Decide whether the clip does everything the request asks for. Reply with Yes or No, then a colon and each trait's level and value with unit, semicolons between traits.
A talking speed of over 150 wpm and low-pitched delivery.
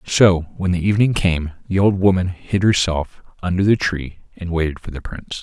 Yes: average, 200 wpm; very low, 90 Hz